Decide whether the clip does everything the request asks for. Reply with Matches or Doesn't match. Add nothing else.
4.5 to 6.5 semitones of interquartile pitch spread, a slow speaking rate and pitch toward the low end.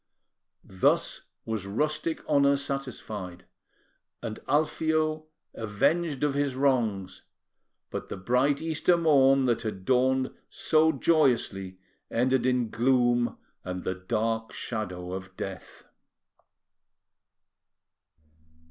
Matches